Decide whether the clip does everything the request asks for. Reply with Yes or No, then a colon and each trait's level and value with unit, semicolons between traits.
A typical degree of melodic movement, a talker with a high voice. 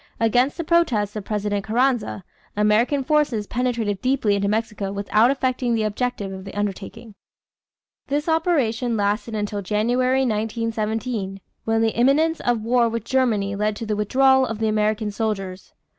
Yes: average, 3.3 semitones; high, 225 Hz